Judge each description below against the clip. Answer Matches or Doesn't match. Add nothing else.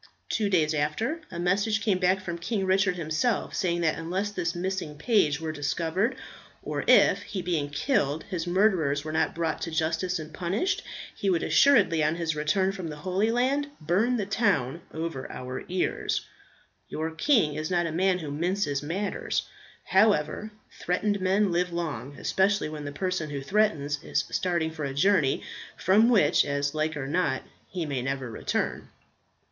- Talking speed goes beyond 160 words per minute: Matches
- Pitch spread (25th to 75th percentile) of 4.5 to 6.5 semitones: Doesn't match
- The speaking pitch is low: Doesn't match